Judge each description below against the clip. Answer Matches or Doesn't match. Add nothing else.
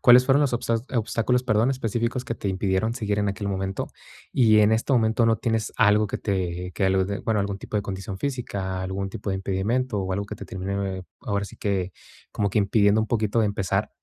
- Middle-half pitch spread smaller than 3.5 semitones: Matches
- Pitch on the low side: Matches